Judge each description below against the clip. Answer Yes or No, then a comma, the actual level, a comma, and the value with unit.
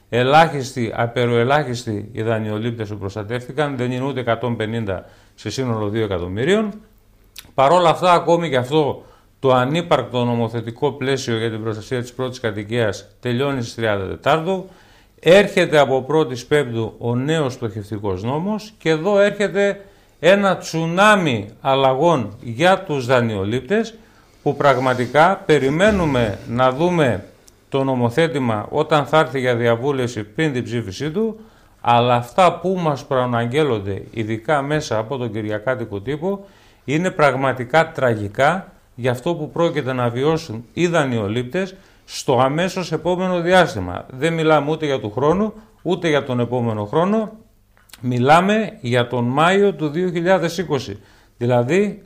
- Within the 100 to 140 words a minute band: Yes, average, 130 wpm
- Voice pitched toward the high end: No, low, 130 Hz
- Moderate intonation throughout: No, wide, 6.0 semitones